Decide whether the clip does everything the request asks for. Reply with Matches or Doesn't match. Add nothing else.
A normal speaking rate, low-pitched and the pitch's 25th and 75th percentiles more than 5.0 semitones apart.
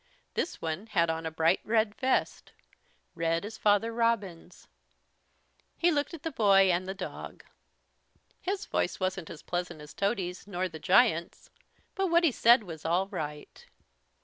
Doesn't match